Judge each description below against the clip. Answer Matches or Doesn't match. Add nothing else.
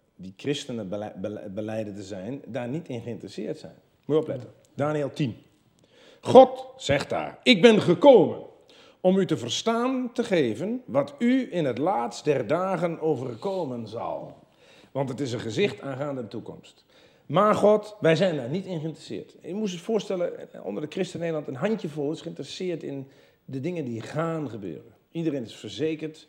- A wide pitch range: Matches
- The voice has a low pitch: Doesn't match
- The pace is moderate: Matches